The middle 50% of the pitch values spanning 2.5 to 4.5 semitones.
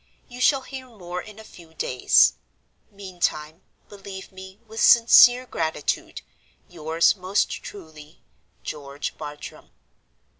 No: average, 5.3 semitones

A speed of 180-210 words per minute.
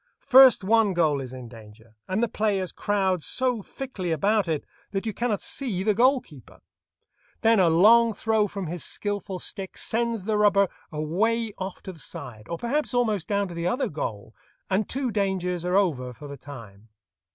Yes: average, 185 wpm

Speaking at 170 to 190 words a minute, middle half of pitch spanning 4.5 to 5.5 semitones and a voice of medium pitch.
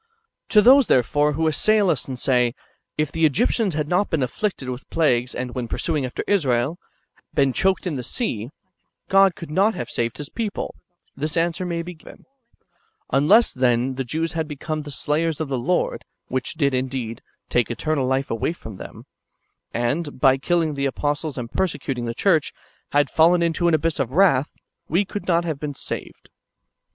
Yes: average, 185 wpm; average, 4.9 semitones; medium, 150 Hz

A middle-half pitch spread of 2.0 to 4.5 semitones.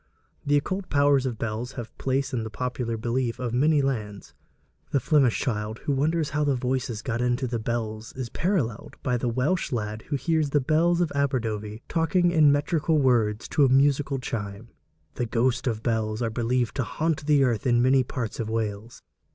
Yes: average, 3.9 semitones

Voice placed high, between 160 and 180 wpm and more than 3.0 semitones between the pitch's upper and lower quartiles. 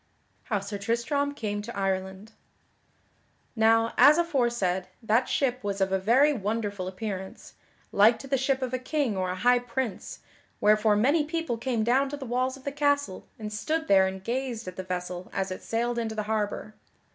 No: high, 225 Hz; average, 190 wpm; average, 4.7 semitones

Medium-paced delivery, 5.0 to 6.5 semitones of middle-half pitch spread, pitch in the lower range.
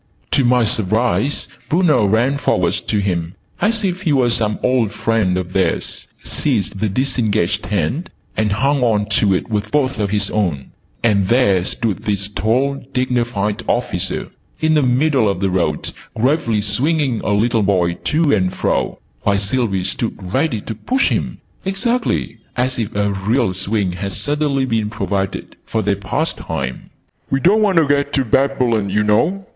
Yes: average, 165 wpm; average, 5.3 semitones; low, 110 Hz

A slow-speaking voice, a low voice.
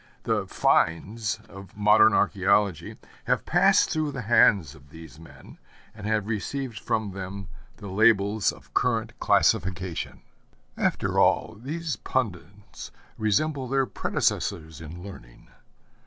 Yes: slow, 120 wpm; low, 100 Hz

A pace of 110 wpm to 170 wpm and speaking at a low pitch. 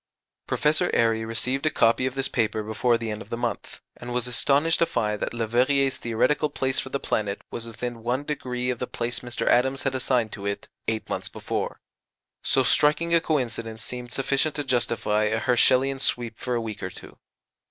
No: average, 195 wpm; low, 125 Hz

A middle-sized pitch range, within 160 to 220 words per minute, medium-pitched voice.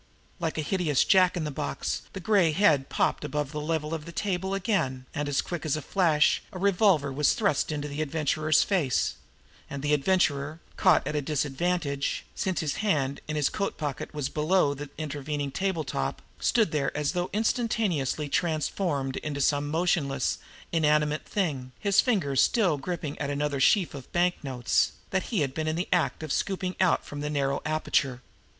Yes: average, 3.9 semitones; average, 180 wpm; medium, 155 Hz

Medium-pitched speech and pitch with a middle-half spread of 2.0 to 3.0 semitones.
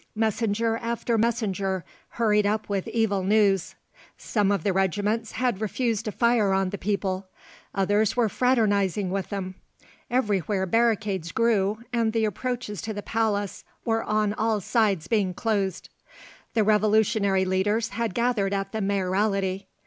No: high, 210 Hz; narrow, 2.5 semitones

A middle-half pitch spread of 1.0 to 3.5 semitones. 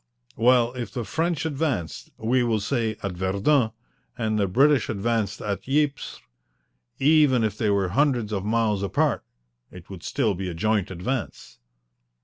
No: average, 4.6 semitones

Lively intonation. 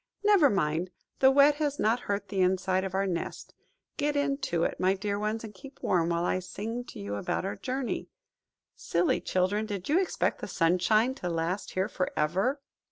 Yes: wide, 6.1 semitones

